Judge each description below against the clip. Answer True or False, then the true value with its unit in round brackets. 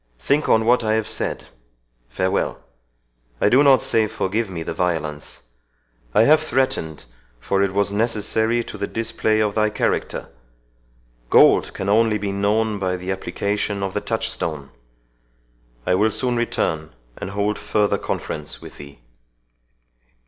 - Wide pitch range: True (5.7 semitones)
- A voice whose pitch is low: True (100 Hz)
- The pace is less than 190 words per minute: True (140 wpm)